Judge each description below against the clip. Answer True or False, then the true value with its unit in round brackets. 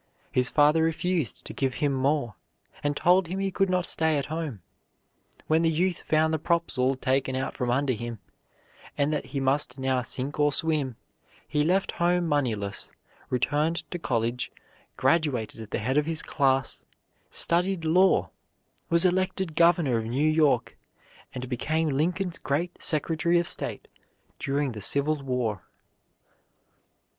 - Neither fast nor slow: True (150 wpm)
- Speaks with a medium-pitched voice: True (150 Hz)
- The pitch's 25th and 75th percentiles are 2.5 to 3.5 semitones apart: False (4.2 semitones)